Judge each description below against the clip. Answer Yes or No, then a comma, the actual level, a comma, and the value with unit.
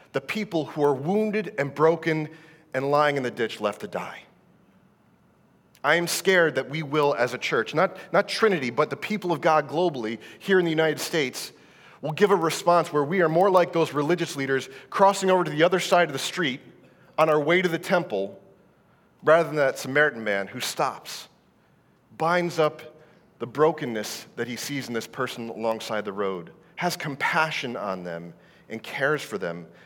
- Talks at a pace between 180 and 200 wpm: Yes, average, 185 wpm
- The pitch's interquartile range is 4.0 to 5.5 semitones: Yes, average, 4.7 semitones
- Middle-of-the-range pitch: Yes, medium, 155 Hz